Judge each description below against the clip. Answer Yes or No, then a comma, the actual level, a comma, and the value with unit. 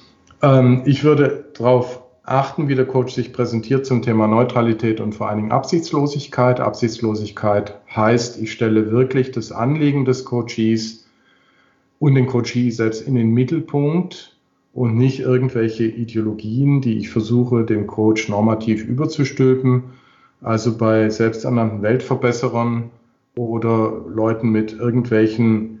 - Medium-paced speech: No, slow, 120 wpm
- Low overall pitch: Yes, low, 120 Hz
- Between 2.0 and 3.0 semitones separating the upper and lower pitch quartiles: Yes, narrow, 2.6 semitones